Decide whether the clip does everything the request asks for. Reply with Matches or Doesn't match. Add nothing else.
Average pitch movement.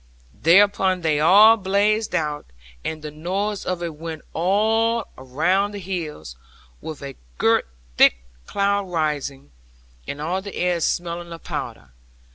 Matches